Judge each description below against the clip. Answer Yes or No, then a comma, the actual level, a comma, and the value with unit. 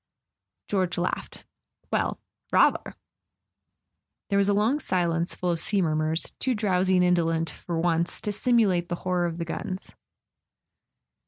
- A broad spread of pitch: No, average, 2.8 semitones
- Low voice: No, medium, 180 Hz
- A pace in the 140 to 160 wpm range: Yes, average, 145 wpm